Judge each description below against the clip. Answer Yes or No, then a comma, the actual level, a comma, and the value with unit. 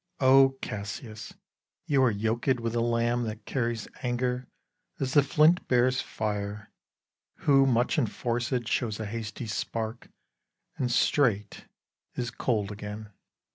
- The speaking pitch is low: Yes, low, 120 Hz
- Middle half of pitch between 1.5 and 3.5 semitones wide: Yes, average, 2.9 semitones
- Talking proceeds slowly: Yes, slow, 125 wpm